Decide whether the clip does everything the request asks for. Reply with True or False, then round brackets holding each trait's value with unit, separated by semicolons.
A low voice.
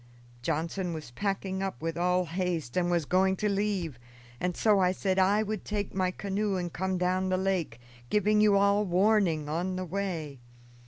False (185 Hz)